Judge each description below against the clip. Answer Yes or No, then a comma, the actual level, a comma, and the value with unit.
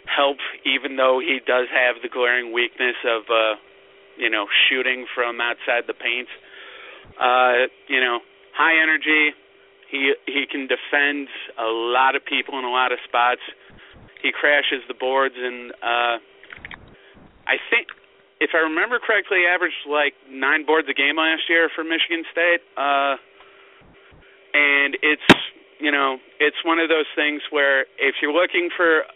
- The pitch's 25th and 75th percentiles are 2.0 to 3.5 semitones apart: No, average, 3.9 semitones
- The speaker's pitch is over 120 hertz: Yes, medium, 140 Hz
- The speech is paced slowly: No, average, 150 wpm